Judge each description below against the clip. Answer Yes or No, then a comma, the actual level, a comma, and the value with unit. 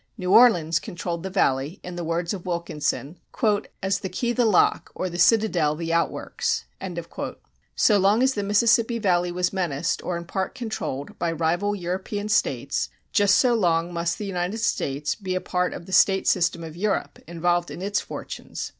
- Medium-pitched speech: Yes, medium, 180 Hz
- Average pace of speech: Yes, average, 180 wpm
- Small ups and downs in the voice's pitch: No, average, 3.3 semitones